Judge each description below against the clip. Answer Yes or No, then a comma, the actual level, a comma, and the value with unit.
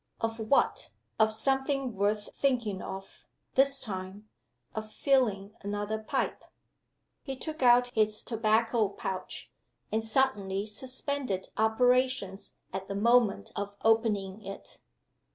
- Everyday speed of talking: No, slow, 115 wpm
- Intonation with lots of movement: No, average, 3.7 semitones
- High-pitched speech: Yes, high, 220 Hz